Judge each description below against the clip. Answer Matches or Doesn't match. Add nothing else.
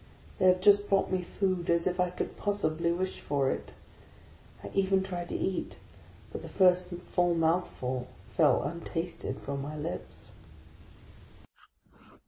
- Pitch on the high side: Doesn't match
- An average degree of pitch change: Doesn't match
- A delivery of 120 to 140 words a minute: Matches